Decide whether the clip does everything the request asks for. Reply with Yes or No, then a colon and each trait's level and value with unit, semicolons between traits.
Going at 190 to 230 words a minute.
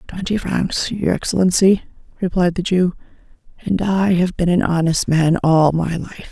No: average, 160 wpm